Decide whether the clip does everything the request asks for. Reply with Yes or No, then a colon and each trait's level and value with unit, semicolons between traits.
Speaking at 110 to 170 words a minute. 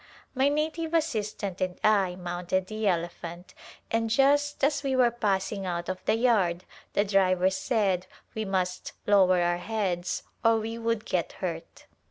Yes: average, 155 wpm